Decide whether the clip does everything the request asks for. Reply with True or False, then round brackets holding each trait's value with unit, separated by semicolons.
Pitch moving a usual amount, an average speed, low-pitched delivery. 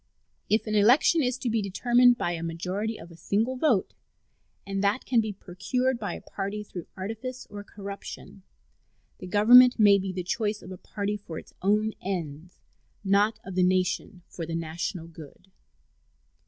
False (3.5 semitones; 170 wpm; 200 Hz)